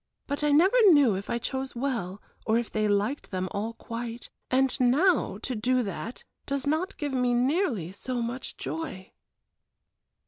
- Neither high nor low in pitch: No, very high, 250 Hz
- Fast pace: No, average, 165 wpm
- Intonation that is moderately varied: Yes, average, 4.5 semitones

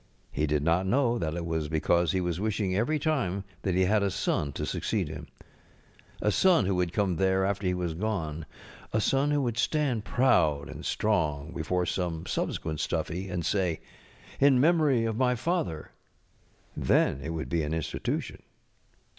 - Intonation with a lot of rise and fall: Yes, wide, 5.8 semitones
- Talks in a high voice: No, very low, 95 Hz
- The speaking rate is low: No, average, 180 wpm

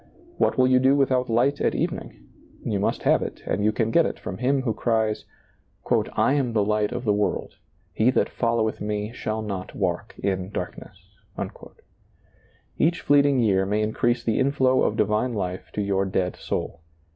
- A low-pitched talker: Yes, low, 110 Hz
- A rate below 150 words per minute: No, average, 185 wpm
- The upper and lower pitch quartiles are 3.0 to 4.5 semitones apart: Yes, average, 3.7 semitones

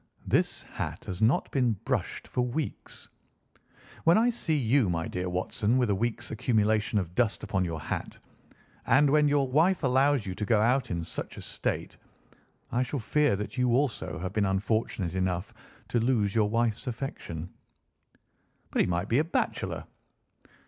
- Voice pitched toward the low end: Yes, low, 115 Hz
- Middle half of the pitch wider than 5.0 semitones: Yes, wide, 5.4 semitones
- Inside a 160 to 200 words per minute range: Yes, average, 170 wpm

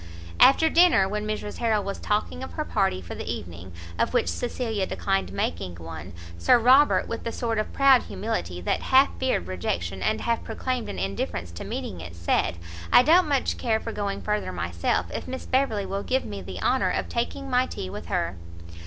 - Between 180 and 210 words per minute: Yes, average, 195 wpm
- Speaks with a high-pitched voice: Yes, high, 200 Hz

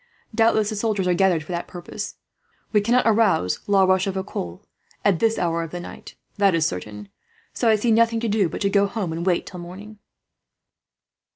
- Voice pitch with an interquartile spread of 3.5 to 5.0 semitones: Yes, average, 3.8 semitones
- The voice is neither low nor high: No, high, 195 Hz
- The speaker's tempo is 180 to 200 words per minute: Yes, average, 190 wpm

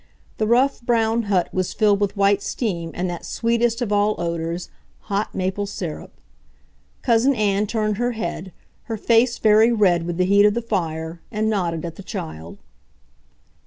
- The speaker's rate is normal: Yes, average, 165 wpm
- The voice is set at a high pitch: Yes, high, 205 Hz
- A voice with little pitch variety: No, average, 4.3 semitones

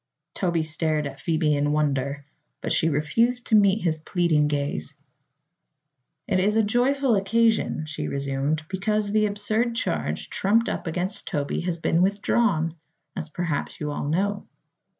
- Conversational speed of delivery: Yes, average, 150 wpm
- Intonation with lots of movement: Yes, wide, 5.7 semitones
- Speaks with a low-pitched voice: No, medium, 175 Hz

